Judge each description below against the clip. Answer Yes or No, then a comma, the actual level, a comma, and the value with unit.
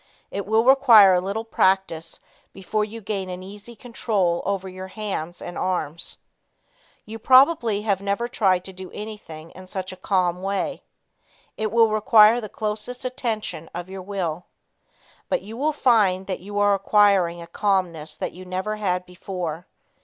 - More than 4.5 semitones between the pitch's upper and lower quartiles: No, average, 2.9 semitones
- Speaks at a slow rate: No, average, 160 wpm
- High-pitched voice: Yes, high, 195 Hz